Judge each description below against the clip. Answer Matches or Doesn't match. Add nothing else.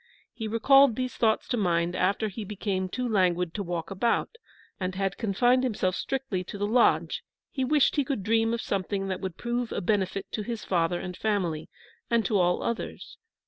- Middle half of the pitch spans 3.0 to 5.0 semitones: Matches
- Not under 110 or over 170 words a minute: Doesn't match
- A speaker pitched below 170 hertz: Doesn't match